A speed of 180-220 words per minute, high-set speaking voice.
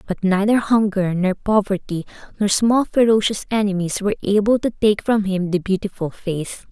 No: average, 160 wpm; high, 200 Hz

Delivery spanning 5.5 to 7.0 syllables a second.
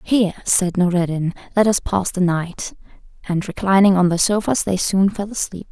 No: 5.0 syllables/s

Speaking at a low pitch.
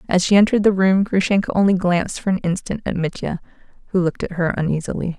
No: medium, 185 Hz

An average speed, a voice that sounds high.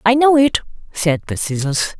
Yes: average, 180 wpm; high, 205 Hz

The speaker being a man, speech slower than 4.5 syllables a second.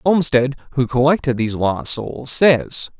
Yes: male; 4.2 syllables/s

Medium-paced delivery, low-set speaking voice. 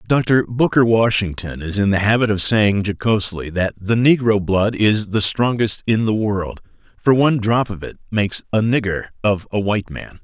Yes: average, 190 wpm; low, 105 Hz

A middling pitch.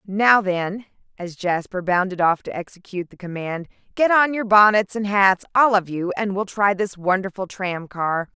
No: high, 195 Hz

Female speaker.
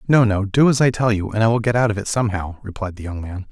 No: male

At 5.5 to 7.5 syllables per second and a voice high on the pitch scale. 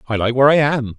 No: 7.1 syllables/s; low, 130 Hz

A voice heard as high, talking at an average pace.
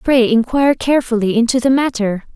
Yes: high, 240 Hz; average, 155 wpm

